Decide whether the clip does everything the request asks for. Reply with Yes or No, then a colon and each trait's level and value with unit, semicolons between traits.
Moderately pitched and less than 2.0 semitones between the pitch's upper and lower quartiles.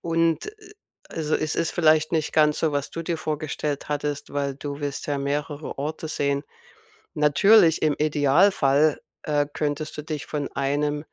Yes: medium, 150 Hz; narrow, 1.6 semitones